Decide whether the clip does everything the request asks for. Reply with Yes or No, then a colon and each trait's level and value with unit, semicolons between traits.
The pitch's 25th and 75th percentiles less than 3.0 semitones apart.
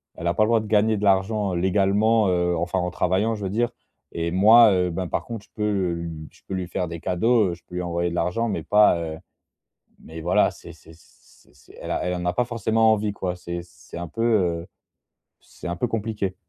No: average, 3.6 semitones